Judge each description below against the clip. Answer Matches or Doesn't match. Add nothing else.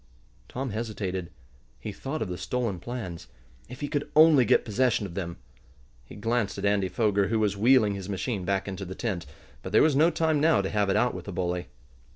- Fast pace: Matches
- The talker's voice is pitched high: Doesn't match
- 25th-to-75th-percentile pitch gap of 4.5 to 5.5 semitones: Matches